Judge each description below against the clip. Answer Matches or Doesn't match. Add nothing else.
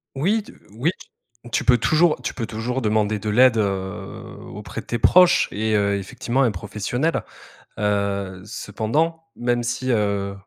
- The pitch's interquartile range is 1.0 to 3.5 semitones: Doesn't match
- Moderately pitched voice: Doesn't match